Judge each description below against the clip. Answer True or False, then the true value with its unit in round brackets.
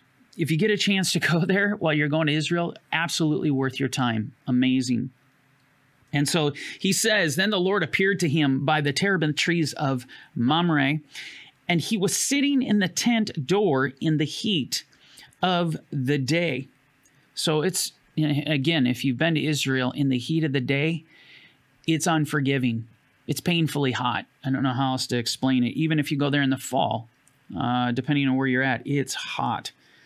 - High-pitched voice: False (150 Hz)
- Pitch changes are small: False (3.8 semitones)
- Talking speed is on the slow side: False (180 wpm)